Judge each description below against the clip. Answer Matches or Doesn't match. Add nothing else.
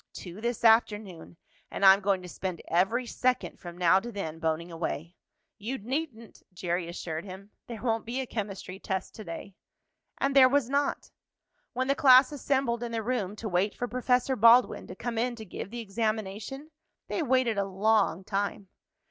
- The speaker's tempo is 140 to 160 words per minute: Doesn't match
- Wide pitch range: Doesn't match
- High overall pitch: Matches